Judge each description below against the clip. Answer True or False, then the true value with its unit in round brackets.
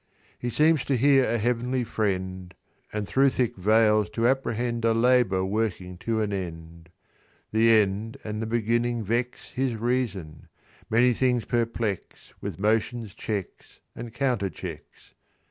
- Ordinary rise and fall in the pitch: True (3.2 semitones)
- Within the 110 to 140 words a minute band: True (135 wpm)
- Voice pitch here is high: False (115 Hz)